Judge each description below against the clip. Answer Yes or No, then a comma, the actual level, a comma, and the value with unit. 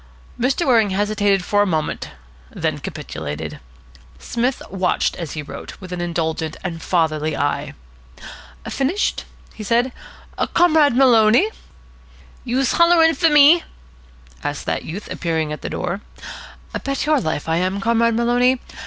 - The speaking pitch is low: No, high, 215 Hz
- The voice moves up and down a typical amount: No, wide, 7.3 semitones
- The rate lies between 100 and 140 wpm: Yes, slow, 135 wpm